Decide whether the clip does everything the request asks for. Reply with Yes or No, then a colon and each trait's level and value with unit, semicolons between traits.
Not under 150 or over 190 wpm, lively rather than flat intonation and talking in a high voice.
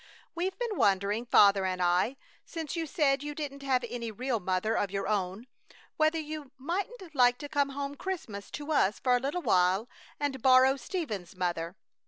Yes: average, 180 wpm; wide, 6.9 semitones; very high, 260 Hz